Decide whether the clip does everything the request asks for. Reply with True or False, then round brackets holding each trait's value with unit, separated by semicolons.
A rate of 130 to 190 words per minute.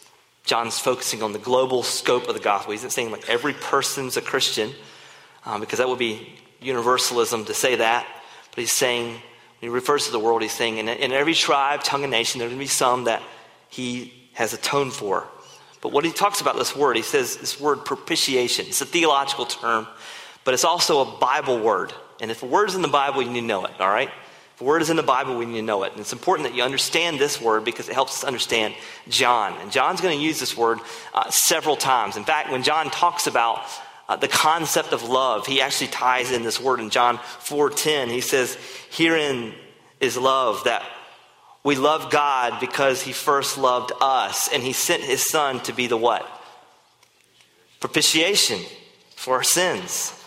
False (205 wpm)